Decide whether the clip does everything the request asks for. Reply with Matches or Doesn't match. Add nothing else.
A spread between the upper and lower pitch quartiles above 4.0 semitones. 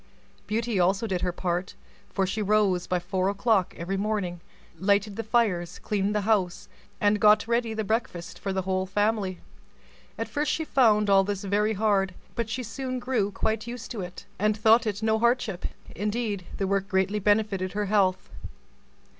Doesn't match